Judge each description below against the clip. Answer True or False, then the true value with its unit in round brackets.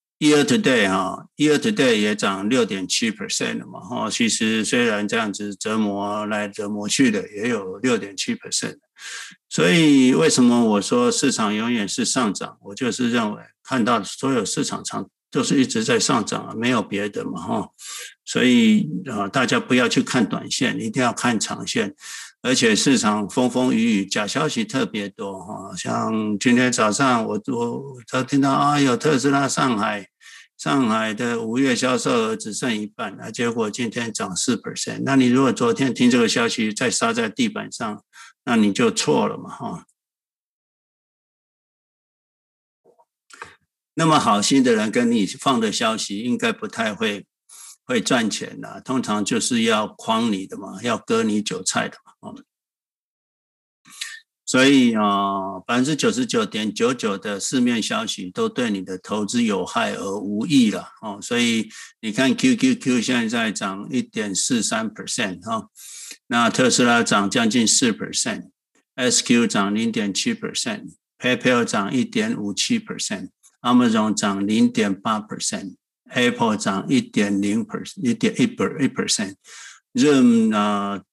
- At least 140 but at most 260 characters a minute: False (285 characters per minute)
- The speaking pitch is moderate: False (225 Hz)